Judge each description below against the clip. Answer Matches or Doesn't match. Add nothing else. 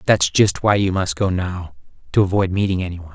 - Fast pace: Matches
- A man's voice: Matches